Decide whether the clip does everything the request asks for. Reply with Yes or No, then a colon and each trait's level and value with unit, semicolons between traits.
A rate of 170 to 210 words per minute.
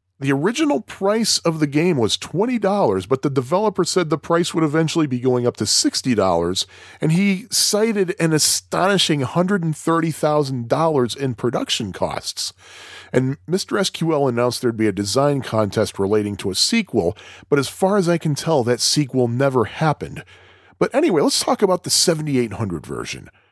No: average, 160 wpm